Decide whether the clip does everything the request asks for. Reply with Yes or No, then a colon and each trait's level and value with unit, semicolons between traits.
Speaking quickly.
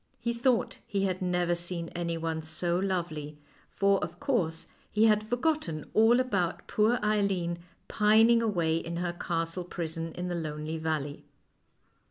No: average, 145 wpm